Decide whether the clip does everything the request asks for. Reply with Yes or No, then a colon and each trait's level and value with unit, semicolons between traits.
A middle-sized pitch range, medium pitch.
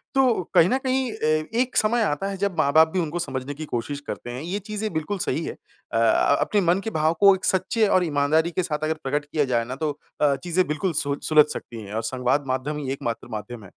No: wide, 5.7 semitones; medium, 155 Hz